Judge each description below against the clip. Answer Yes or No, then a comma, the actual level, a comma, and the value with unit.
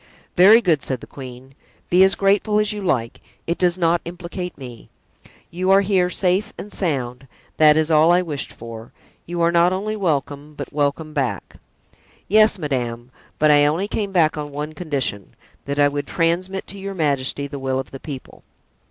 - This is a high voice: No, medium, 160 Hz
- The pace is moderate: Yes, average, 180 wpm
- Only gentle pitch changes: No, average, 4.7 semitones